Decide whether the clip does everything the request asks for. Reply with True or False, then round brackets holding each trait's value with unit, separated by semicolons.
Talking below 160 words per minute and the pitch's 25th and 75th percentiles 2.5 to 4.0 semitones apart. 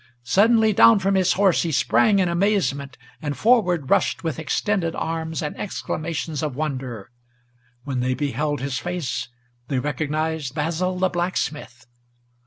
False (140 wpm; 4.6 semitones)